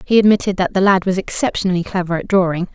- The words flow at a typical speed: No, fast, 220 wpm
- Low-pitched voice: No, medium, 185 Hz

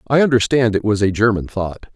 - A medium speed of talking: No, fast, 215 wpm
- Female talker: No, male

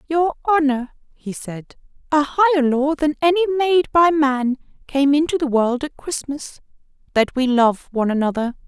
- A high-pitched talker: Yes, very high, 285 Hz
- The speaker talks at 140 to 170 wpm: Yes, average, 150 wpm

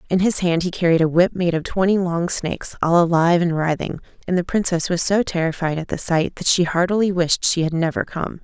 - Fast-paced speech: Yes, fast, 235 wpm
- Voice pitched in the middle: Yes, medium, 175 Hz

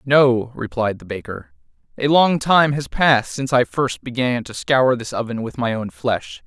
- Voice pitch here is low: Yes, low, 130 Hz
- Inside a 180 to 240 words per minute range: Yes, average, 195 wpm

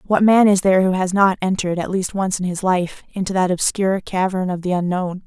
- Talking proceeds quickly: Yes, fast, 240 wpm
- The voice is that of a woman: Yes, female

